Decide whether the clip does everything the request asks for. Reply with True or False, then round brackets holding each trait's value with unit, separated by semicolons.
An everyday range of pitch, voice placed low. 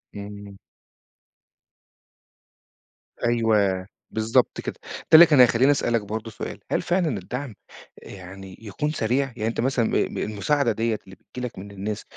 True (3.7 semitones; 110 Hz)